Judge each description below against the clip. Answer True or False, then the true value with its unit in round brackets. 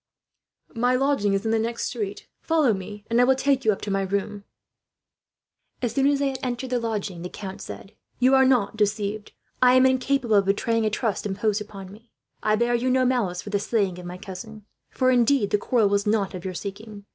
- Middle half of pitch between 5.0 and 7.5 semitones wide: False (3.8 semitones)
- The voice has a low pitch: False (220 Hz)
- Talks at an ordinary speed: False (220 wpm)